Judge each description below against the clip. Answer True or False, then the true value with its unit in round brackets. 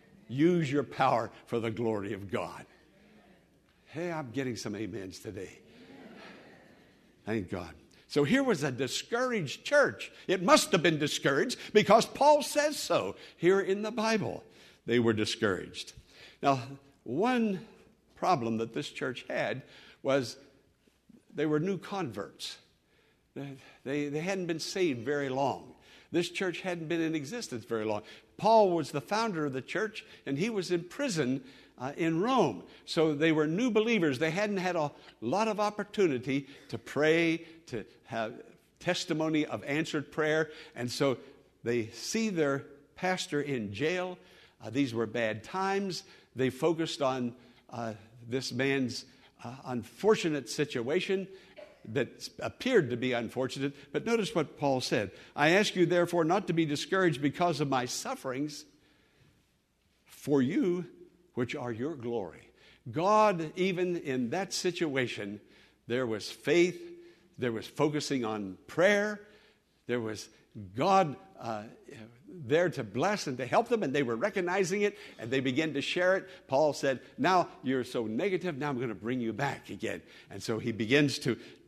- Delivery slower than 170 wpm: True (150 wpm)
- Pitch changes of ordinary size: False (6.4 semitones)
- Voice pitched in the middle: True (150 Hz)